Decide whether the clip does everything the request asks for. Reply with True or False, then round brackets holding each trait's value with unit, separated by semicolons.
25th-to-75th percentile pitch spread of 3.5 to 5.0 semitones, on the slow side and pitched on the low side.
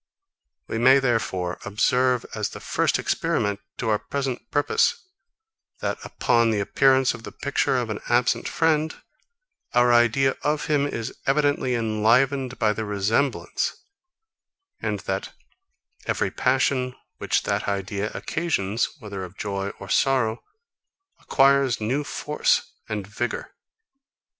True (4.2 semitones; 125 wpm; 120 Hz)